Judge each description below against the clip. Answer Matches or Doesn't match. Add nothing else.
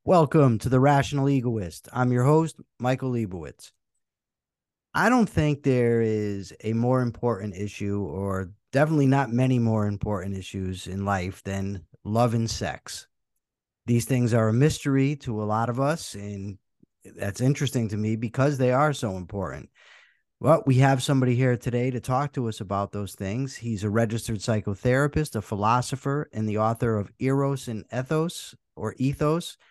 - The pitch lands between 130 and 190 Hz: Doesn't match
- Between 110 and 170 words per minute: Matches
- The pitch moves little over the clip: Doesn't match